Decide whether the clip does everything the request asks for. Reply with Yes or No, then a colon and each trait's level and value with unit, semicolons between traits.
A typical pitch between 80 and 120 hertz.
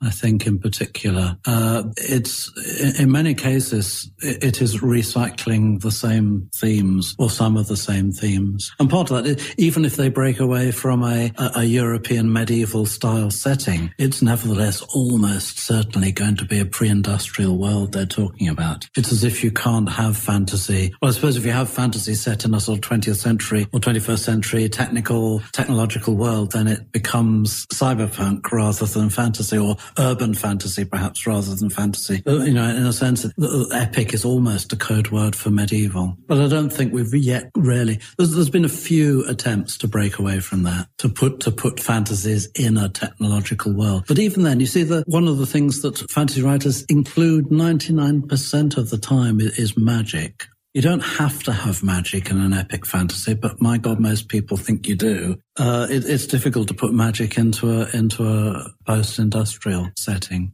Yes: low, 115 Hz